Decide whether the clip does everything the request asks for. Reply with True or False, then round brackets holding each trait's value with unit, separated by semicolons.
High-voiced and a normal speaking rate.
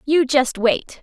True (265 Hz; 175 wpm)